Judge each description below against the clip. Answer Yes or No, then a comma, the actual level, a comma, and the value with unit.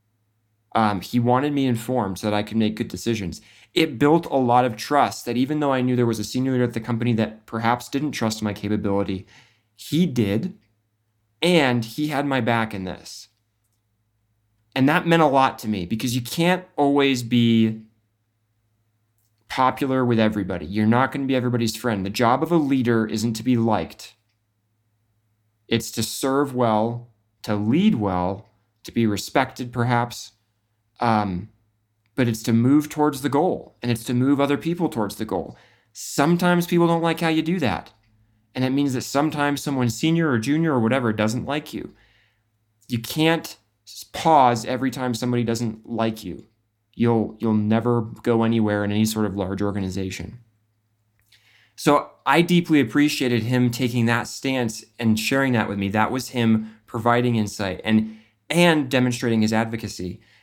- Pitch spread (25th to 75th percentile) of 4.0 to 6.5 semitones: No, average, 3.0 semitones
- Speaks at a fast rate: No, average, 170 wpm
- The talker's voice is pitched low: Yes, low, 115 Hz